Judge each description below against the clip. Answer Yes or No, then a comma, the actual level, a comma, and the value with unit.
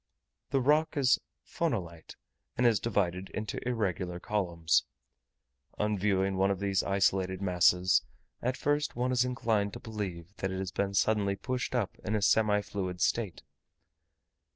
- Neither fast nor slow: Yes, average, 150 wpm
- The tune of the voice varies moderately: Yes, average, 3.9 semitones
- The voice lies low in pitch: Yes, low, 100 Hz